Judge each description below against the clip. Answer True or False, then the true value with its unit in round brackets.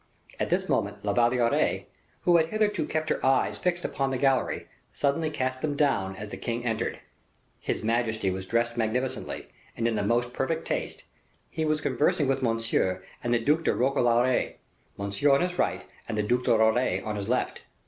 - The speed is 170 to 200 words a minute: True (190 wpm)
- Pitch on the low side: True (125 Hz)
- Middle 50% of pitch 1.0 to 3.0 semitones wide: False (4.0 semitones)